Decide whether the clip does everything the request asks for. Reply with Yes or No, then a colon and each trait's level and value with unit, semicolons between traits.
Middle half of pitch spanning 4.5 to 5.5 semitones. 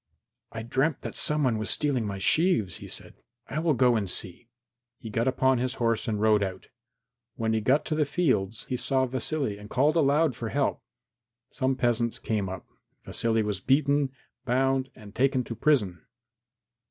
No: average, 4.0 semitones